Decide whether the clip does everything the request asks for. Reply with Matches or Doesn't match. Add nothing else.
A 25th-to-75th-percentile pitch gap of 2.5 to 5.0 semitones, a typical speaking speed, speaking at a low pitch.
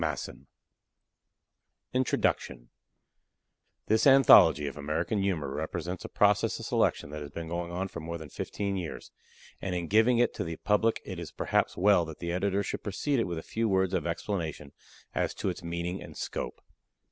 Matches